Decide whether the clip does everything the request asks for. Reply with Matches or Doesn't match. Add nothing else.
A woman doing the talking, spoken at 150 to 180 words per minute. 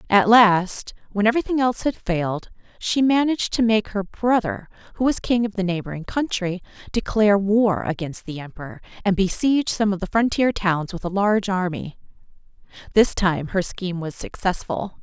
Matches